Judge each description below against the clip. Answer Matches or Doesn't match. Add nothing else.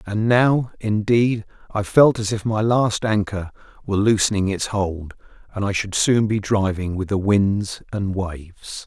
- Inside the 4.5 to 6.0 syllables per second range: Doesn't match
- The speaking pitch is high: Doesn't match